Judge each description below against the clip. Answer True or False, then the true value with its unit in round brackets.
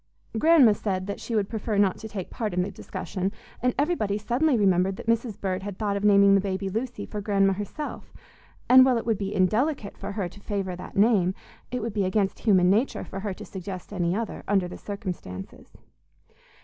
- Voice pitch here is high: True (200 Hz)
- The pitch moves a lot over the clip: False (2.8 semitones)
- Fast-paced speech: True (210 wpm)